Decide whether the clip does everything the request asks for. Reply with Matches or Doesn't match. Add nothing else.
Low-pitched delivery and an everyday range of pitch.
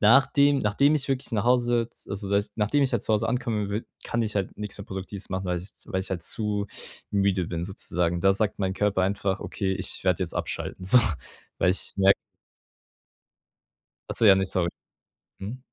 Matches